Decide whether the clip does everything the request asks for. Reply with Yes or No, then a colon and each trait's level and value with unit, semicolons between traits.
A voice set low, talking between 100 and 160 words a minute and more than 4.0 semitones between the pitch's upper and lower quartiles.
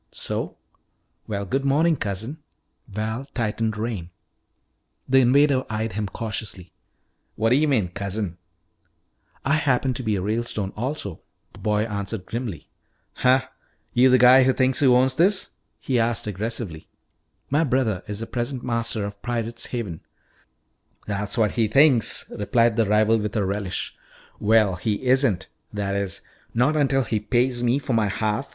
No: low, 115 Hz; average, 155 wpm; average, 3.7 semitones